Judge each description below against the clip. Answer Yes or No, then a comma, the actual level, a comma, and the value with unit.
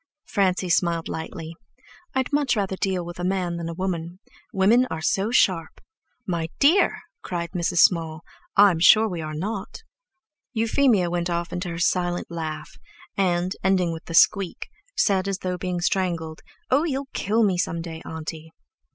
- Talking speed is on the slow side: No, average, 160 wpm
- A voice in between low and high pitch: Yes, medium, 180 Hz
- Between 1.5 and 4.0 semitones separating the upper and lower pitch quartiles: Yes, average, 2.8 semitones